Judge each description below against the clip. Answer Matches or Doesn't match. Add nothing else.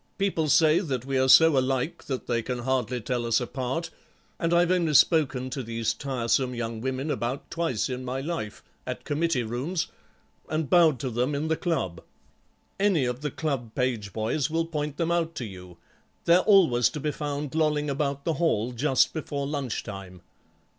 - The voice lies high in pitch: Doesn't match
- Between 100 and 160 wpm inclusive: Doesn't match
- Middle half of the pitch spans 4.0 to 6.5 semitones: Matches